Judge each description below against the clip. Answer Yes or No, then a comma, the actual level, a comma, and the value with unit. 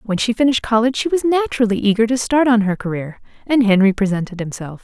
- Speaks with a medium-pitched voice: No, high, 225 Hz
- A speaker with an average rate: No, fast, 210 wpm